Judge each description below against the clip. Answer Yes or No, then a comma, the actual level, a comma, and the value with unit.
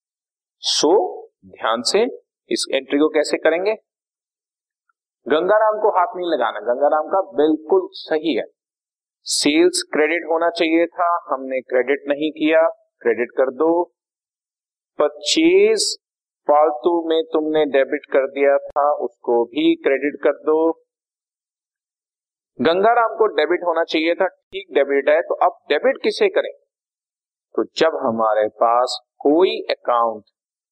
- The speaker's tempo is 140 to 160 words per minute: No, average, 125 wpm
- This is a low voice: No, medium, 170 Hz